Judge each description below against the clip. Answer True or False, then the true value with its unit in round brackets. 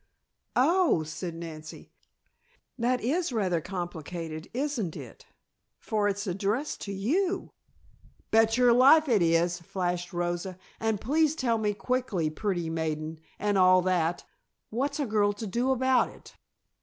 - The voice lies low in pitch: False (205 Hz)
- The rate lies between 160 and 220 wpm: False (135 wpm)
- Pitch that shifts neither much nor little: False (6.3 semitones)